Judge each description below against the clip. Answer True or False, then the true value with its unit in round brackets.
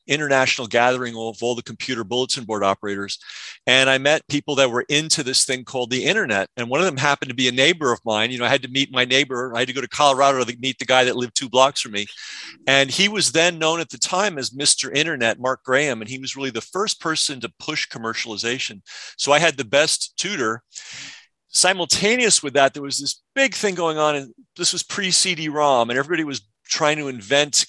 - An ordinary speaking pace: False (230 wpm)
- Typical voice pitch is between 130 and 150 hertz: True (135 Hz)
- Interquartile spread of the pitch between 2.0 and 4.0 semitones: True (3.3 semitones)